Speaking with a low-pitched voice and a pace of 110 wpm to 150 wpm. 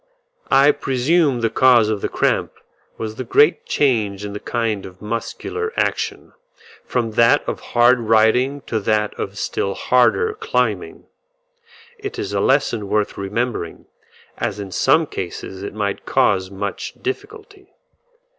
Yes: low, 115 Hz; average, 140 wpm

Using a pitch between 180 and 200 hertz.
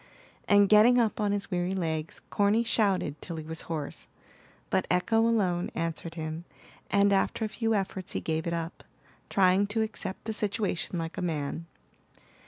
Yes: high, 190 Hz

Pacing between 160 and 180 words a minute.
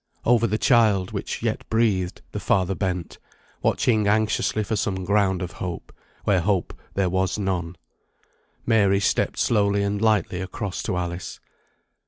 No: average, 145 wpm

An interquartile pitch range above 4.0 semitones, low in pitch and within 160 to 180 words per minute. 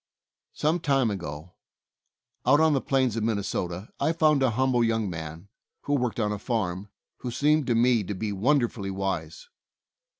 Yes: wide, 5.6 semitones; low, 115 Hz; average, 170 wpm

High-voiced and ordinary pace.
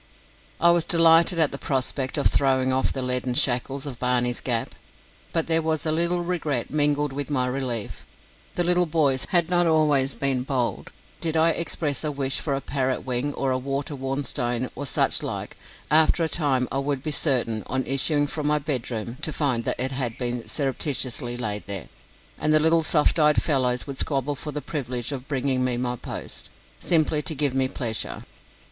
No: medium, 140 Hz; average, 190 wpm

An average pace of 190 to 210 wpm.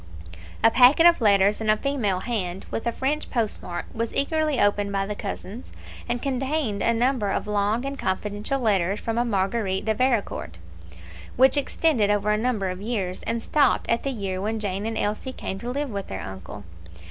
Yes: average, 195 wpm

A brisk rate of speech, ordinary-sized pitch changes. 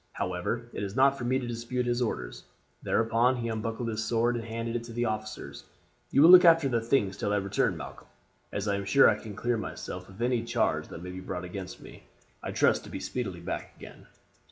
Yes: fast, 225 wpm; average, 3.2 semitones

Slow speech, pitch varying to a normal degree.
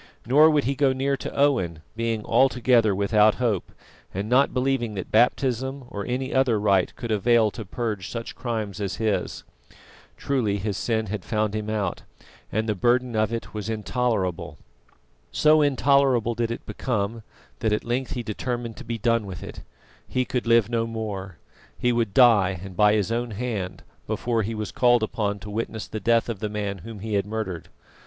No: average, 185 wpm; average, 3.0 semitones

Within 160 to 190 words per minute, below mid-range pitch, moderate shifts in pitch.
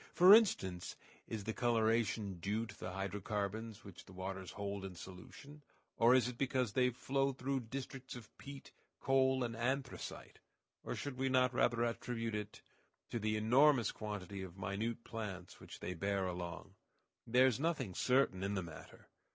Yes: average, 165 wpm; low, 115 Hz; average, 4.7 semitones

